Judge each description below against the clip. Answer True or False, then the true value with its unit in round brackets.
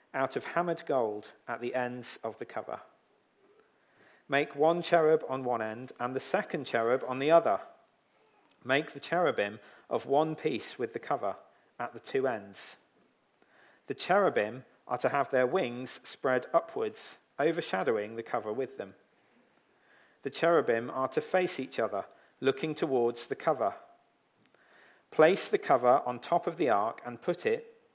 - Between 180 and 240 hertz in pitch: False (135 Hz)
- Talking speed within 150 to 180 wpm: True (155 wpm)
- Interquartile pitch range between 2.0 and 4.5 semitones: False (5.2 semitones)